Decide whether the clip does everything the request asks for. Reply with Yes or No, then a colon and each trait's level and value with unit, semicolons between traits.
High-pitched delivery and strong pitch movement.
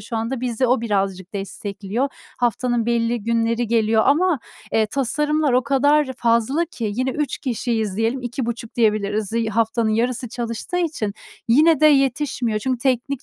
No: high, 235 Hz; average, 3.1 semitones